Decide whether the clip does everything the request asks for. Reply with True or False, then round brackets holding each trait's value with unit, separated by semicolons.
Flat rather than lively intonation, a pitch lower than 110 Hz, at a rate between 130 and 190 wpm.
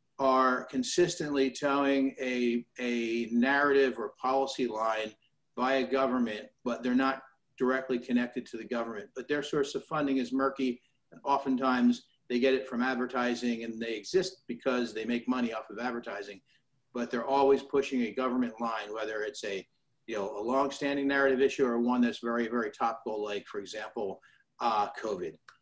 False (2.2 semitones; 125 Hz; 165 wpm)